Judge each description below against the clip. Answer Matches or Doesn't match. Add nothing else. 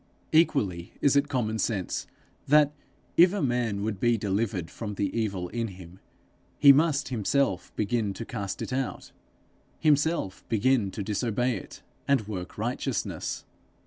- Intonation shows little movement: Doesn't match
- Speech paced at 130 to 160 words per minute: Matches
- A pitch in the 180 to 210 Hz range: Doesn't match